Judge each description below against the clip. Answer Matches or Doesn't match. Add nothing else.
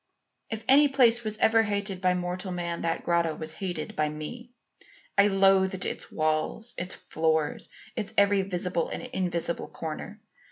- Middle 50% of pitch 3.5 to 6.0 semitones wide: Matches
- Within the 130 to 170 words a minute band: Matches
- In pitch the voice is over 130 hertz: Matches